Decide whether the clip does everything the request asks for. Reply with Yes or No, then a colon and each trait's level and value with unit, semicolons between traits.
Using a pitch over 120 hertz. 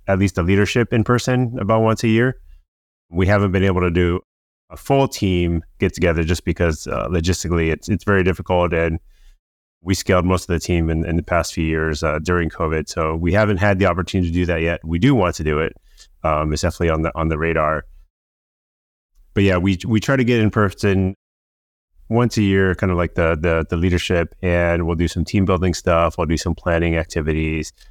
No: very low, 85 Hz